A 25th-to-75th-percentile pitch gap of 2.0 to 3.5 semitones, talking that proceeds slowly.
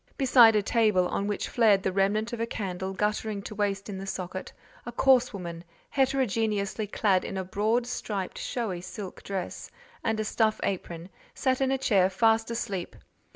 No: average, 3.1 semitones; average, 175 wpm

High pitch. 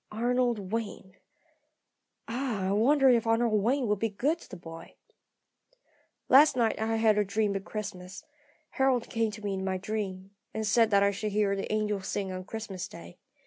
Yes: high, 215 Hz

